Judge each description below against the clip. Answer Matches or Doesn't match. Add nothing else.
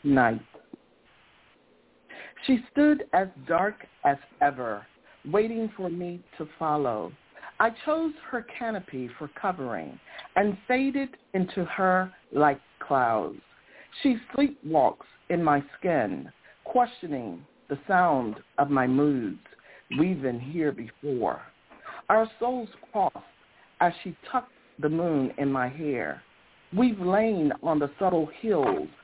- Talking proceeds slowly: Matches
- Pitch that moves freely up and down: Matches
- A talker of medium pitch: Matches